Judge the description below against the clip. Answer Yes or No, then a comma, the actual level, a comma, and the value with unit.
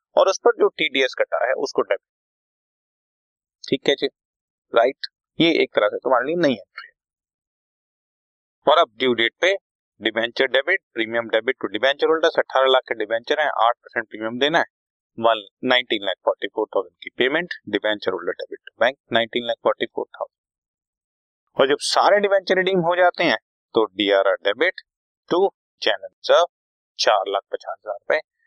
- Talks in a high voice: No, low, 135 Hz